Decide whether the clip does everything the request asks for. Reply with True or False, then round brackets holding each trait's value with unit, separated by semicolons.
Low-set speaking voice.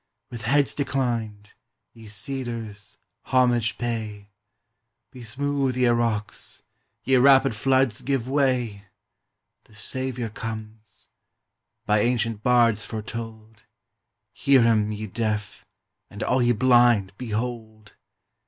True (115 Hz)